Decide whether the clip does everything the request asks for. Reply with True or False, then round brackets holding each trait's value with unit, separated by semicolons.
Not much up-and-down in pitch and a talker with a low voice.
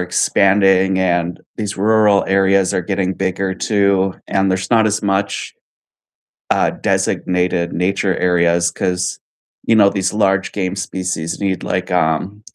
True (1.5 semitones; 95 Hz)